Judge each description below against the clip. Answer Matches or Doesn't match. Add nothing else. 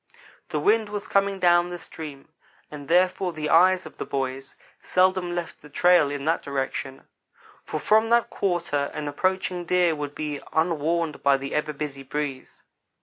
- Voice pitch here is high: Doesn't match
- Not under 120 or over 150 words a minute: Doesn't match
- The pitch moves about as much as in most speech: Matches